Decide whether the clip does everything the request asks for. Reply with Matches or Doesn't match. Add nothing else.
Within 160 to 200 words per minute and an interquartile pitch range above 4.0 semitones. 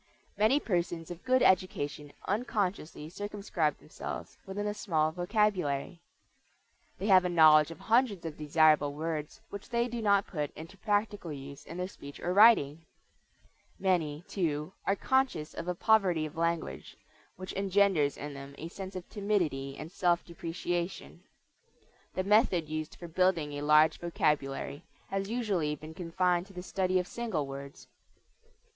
Doesn't match